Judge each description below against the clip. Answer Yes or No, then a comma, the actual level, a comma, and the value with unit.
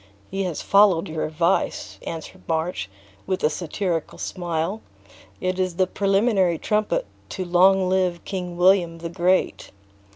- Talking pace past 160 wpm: No, slow, 135 wpm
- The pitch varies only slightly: Yes, narrow, 2.3 semitones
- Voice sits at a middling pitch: Yes, medium, 180 Hz